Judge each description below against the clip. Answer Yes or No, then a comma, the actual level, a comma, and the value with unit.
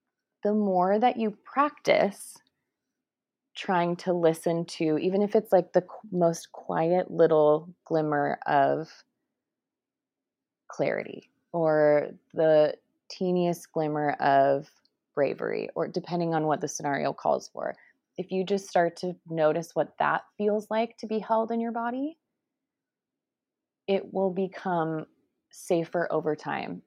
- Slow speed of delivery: Yes, slow, 125 wpm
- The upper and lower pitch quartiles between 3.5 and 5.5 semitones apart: Yes, average, 4.8 semitones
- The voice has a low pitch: No, medium, 180 Hz